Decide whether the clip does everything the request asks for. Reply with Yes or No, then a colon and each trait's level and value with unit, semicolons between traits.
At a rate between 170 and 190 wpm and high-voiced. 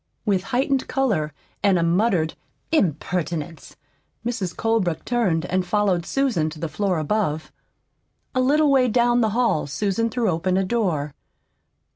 No: average, 140 wpm; high, 195 Hz